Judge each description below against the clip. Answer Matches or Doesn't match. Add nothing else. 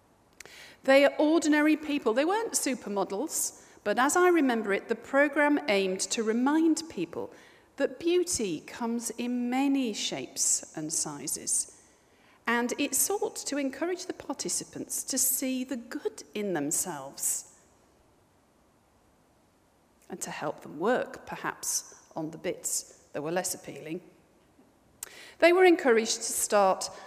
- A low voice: Doesn't match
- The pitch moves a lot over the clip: Matches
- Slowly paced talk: Matches